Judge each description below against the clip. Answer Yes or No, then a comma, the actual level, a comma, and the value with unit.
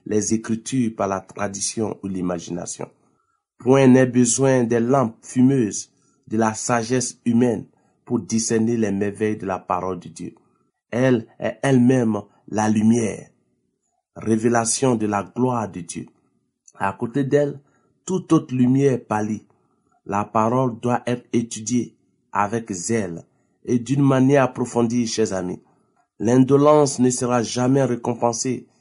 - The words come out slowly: Yes, slow, 130 wpm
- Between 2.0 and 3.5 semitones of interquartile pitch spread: Yes, average, 3.1 semitones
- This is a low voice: Yes, low, 120 Hz